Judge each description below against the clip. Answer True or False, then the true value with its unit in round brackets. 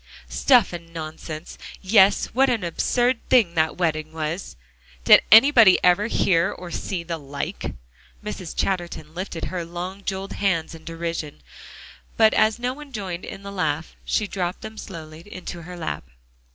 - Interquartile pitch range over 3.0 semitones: True (3.7 semitones)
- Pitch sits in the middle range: True (180 Hz)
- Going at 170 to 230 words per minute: False (155 wpm)